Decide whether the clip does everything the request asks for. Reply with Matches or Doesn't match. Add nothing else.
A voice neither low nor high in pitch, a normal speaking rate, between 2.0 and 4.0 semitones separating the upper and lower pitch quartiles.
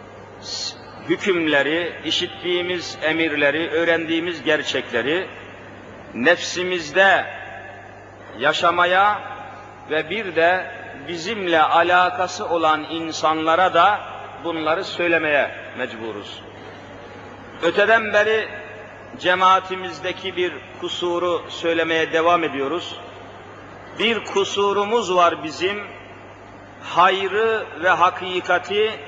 Doesn't match